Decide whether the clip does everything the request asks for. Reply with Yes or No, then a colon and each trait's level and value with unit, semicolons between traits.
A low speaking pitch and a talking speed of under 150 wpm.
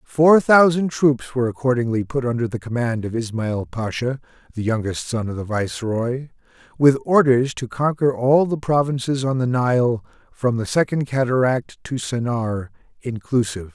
No: low, 125 Hz; average, 155 wpm